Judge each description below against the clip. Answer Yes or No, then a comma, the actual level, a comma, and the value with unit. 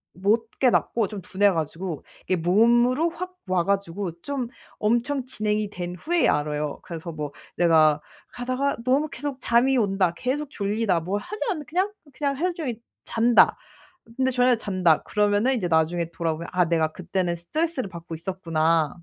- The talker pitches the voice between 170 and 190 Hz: No, high, 205 Hz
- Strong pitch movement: Yes, wide, 7.1 semitones